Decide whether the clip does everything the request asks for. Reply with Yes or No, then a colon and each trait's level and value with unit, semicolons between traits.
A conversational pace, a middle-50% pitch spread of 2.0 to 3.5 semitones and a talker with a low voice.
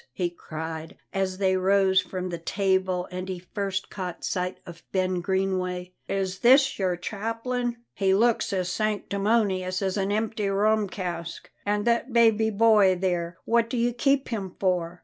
No: average, 160 wpm; average, 3.0 semitones; high, 190 Hz